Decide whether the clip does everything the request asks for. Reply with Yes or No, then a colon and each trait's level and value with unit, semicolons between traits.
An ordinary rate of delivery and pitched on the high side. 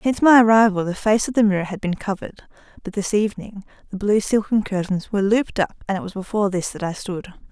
No: fast, 230 wpm; high, 205 Hz